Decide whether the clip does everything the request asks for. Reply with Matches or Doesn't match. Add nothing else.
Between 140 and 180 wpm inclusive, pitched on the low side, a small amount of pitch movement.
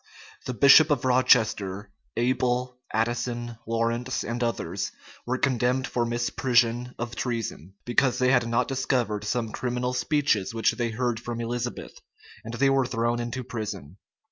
Matches